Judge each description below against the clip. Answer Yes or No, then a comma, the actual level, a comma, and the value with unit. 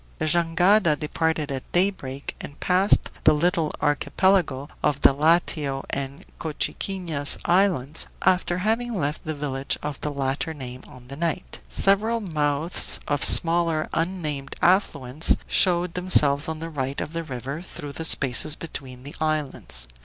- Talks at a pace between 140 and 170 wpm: Yes, average, 145 wpm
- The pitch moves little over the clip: No, average, 3.9 semitones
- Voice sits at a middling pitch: Yes, medium, 155 Hz